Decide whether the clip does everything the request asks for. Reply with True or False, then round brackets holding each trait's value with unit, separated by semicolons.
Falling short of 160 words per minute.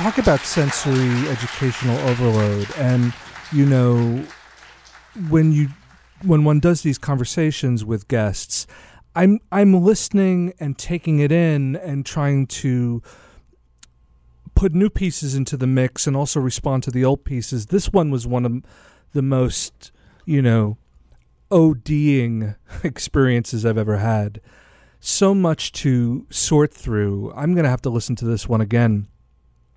True (140 wpm)